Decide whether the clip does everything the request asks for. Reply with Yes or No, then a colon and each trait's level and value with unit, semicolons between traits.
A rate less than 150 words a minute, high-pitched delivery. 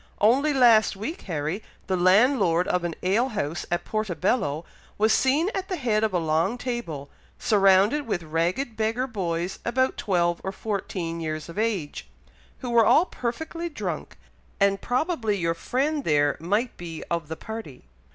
No: average, 160 wpm; high, 205 Hz